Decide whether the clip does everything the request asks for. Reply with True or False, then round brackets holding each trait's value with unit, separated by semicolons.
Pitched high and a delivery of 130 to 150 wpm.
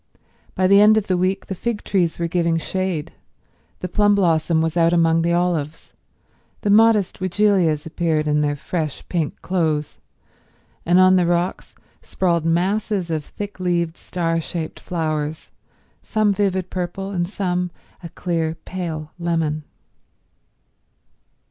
False (175 Hz; 140 wpm)